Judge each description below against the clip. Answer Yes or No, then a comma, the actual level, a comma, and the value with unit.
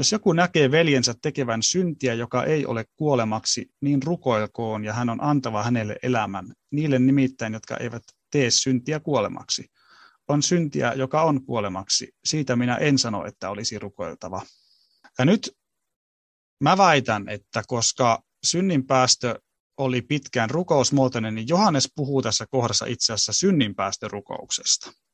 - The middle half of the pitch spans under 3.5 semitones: No, average, 4.4 semitones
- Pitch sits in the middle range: No, low, 125 Hz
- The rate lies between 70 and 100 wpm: No, average, 130 wpm